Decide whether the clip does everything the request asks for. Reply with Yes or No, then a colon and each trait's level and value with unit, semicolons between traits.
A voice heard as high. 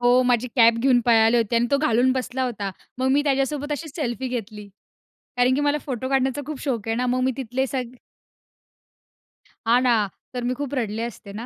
Yes: very high, 250 Hz